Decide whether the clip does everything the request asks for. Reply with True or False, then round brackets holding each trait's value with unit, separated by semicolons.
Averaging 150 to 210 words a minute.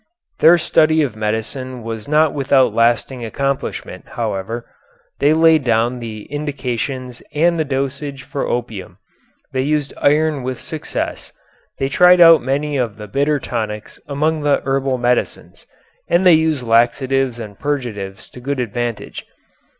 False (140 wpm)